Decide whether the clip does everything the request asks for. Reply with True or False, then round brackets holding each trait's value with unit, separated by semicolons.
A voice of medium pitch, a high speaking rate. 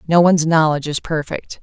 False (160 Hz; 185 wpm)